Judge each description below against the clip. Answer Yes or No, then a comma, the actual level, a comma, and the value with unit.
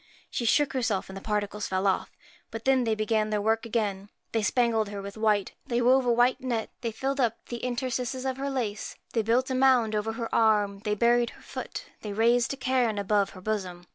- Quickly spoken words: Yes, fast, 220 wpm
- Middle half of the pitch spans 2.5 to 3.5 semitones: Yes, average, 2.9 semitones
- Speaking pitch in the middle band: No, high, 225 Hz